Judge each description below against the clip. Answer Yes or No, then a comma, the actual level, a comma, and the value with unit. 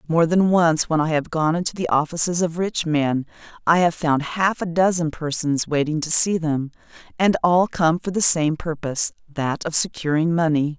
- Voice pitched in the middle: Yes, medium, 160 Hz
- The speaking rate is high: No, average, 195 wpm